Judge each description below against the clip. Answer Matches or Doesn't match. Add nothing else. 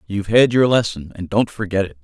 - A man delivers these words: Matches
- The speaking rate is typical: Doesn't match